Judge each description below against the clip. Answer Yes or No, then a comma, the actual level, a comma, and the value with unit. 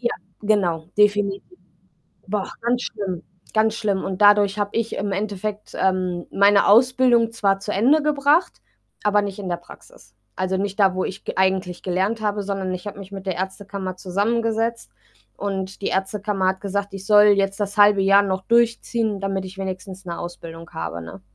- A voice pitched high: Yes, high, 200 Hz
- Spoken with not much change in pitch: Yes, narrow, 1.9 semitones